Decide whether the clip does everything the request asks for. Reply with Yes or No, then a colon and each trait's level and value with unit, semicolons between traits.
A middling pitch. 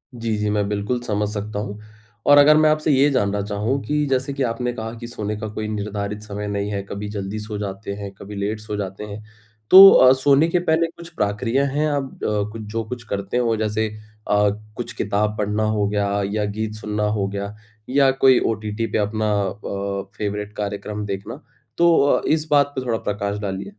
No: low, 105 Hz